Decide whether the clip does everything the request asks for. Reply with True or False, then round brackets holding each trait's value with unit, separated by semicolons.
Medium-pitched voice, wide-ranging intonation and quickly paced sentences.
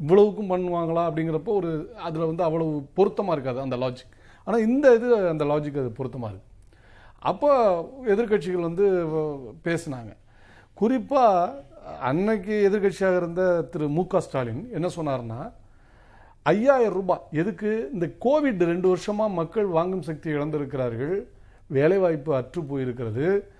False (170 Hz; 6.2 semitones; 120 wpm)